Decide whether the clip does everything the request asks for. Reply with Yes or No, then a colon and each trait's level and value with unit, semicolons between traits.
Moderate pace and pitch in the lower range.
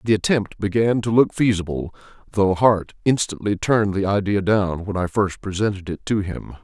Yes: average, 180 wpm; low, 100 Hz